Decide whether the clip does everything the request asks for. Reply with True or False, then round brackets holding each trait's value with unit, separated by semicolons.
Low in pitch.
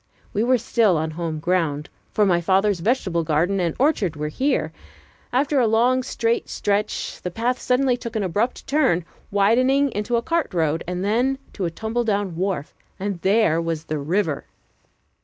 False (200 Hz)